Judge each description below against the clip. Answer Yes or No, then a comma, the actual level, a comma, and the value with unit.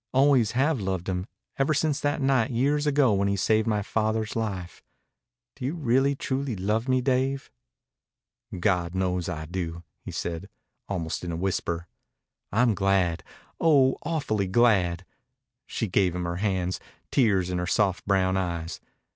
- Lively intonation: Yes, wide, 6.3 semitones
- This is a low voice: Yes, low, 100 Hz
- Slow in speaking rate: No, average, 155 wpm